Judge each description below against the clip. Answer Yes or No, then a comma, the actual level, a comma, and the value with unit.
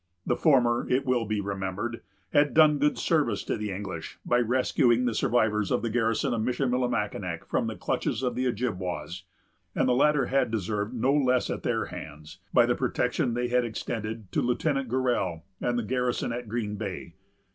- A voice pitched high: No, low, 120 Hz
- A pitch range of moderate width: Yes, average, 3.3 semitones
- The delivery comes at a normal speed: Yes, average, 180 wpm